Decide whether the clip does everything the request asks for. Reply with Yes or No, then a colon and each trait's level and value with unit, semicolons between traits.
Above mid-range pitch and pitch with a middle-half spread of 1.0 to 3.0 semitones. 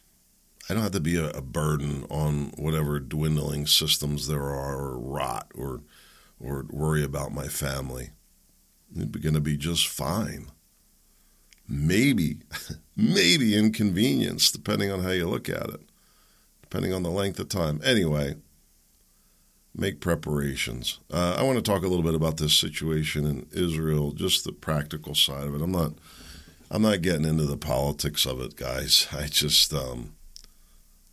No: very low, 75 Hz; narrow, 2.4 semitones